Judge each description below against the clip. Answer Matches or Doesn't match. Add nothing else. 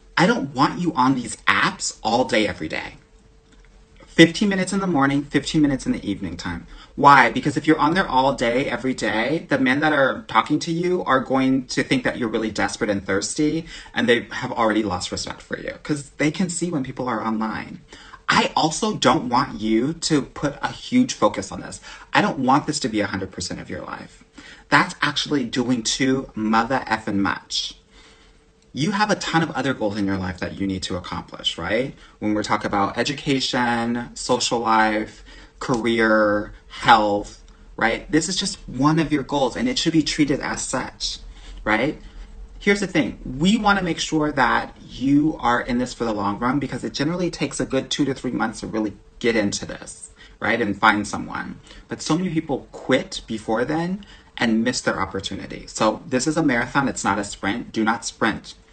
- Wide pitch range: Matches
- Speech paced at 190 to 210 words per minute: Matches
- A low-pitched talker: Matches